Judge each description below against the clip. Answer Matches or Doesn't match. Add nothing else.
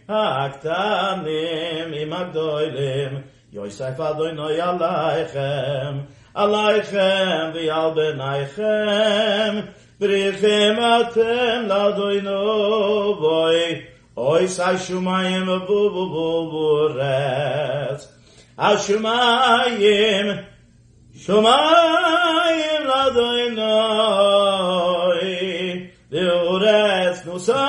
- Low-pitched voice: Doesn't match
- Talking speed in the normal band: Doesn't match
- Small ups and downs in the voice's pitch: Doesn't match